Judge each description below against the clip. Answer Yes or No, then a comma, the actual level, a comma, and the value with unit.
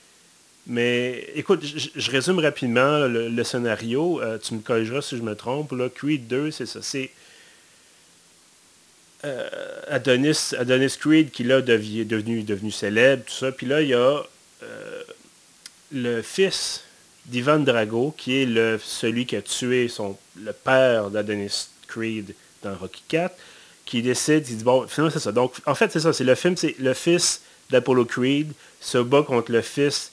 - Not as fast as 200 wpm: Yes, average, 170 wpm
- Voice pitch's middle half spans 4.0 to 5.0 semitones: Yes, average, 4.6 semitones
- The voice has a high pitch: No, low, 130 Hz